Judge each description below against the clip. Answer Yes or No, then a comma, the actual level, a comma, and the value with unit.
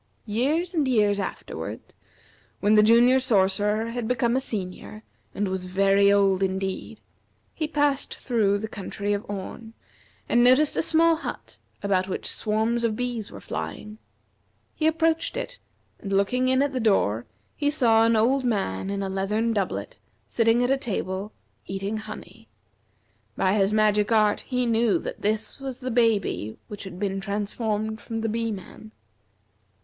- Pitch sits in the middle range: No, high, 220 Hz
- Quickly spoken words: No, average, 155 wpm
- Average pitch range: Yes, average, 3.6 semitones